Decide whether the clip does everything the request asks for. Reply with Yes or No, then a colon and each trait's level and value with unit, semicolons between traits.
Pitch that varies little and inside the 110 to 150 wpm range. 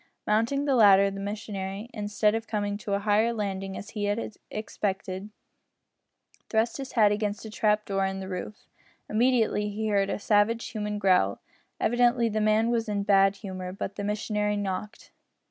No: narrow, 1.7 semitones; average, 175 wpm